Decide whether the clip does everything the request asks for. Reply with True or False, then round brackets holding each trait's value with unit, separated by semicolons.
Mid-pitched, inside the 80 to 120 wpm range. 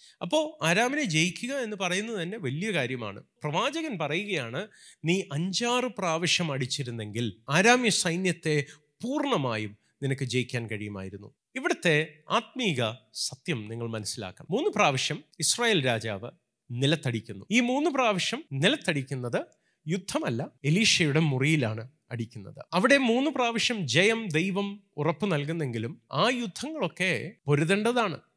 True (165 Hz; 100 wpm)